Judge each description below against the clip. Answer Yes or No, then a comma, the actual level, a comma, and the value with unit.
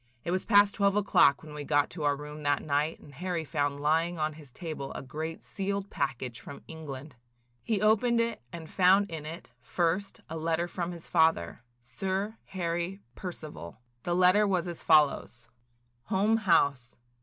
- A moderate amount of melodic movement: Yes, average, 4.6 semitones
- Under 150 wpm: No, average, 175 wpm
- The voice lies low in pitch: No, medium, 165 Hz